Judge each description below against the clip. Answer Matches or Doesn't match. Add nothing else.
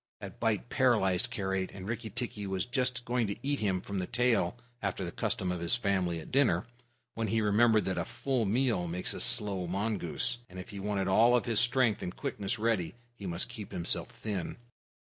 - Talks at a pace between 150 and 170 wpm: Doesn't match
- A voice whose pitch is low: Matches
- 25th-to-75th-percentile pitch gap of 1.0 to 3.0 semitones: Doesn't match